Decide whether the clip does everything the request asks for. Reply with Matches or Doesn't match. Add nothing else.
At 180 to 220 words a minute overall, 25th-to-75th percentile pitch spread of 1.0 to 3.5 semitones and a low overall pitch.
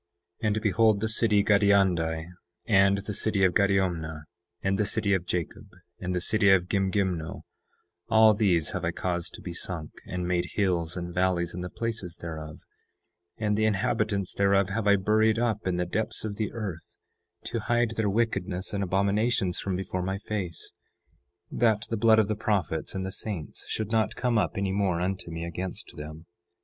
Matches